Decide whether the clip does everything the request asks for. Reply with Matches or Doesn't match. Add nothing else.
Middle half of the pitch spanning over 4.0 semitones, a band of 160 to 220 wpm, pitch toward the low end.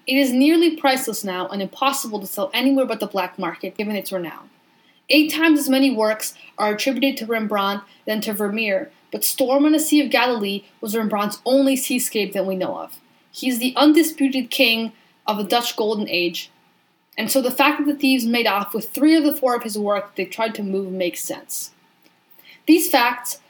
Doesn't match